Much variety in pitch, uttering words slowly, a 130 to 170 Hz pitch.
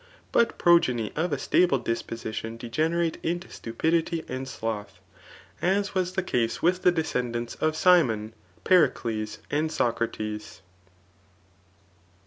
Yes: wide, 7.0 semitones; slow, 115 wpm; medium, 140 Hz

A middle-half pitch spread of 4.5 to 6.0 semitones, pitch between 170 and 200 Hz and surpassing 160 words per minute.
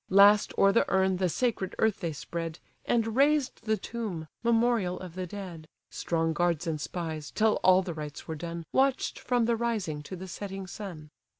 Yes: average, 4.9 semitones; high, 190 Hz; average, 185 wpm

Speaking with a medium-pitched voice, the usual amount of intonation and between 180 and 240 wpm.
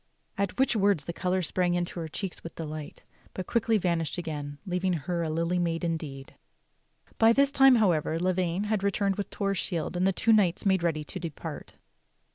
Yes: medium, 180 Hz; average, 3.2 semitones; average, 190 wpm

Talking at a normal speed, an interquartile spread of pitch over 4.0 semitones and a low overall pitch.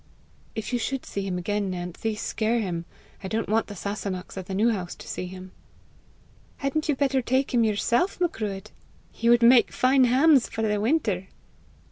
No: average, 180 wpm; average, 4.8 semitones; high, 220 Hz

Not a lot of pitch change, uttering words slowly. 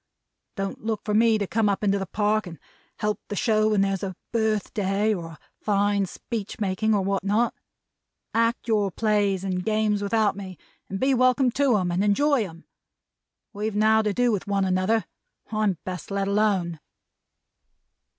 No: narrow, 2.0 semitones; average, 170 wpm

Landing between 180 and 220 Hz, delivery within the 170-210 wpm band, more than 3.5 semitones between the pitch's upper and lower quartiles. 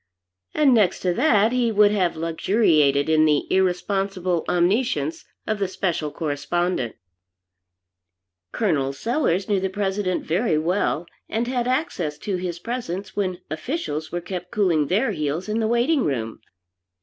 No: medium, 185 Hz; average, 140 wpm; average, 5.0 semitones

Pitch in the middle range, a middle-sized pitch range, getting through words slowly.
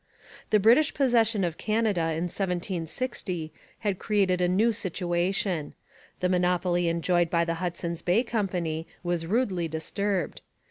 Yes: medium, 180 Hz; average, 3.4 semitones; slow, 130 wpm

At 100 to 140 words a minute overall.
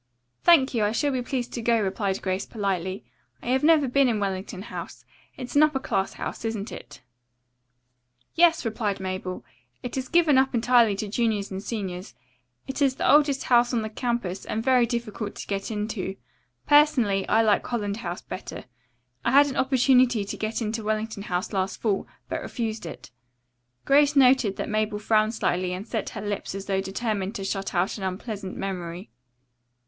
No: average, 185 wpm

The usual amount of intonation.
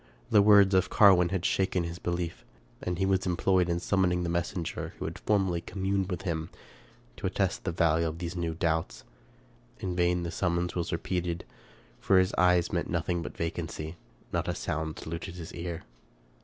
No: narrow, 1.8 semitones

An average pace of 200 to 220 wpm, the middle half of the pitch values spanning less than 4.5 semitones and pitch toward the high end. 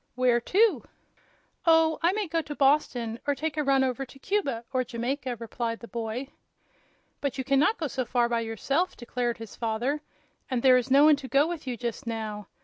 Yes: fast, 205 wpm; average, 3.9 semitones; very high, 260 Hz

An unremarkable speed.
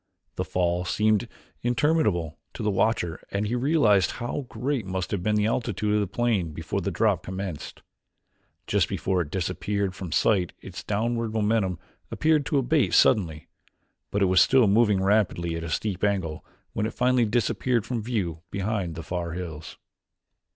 Yes: average, 165 wpm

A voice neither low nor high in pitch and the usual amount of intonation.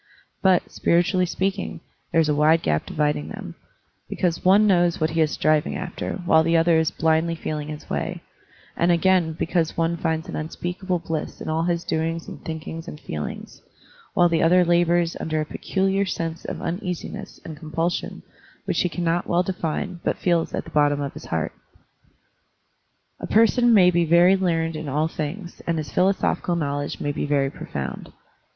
No: medium, 165 Hz; narrow, 2.2 semitones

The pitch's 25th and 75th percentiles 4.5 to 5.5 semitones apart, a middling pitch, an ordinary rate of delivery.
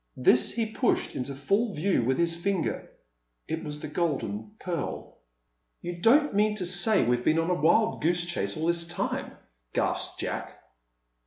Yes: average, 4.8 semitones; medium, 170 Hz; average, 165 wpm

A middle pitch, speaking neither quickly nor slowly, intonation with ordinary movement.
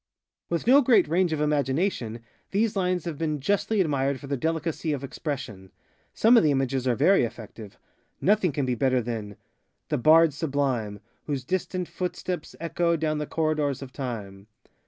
Yes: medium, 150 Hz; average, 165 wpm; average, 4.8 semitones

